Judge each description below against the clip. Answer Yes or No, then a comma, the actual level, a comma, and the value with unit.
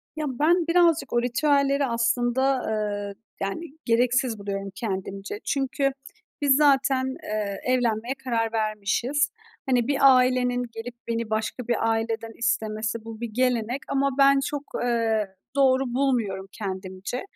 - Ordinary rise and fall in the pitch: Yes, average, 3.6 semitones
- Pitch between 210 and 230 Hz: No, high, 240 Hz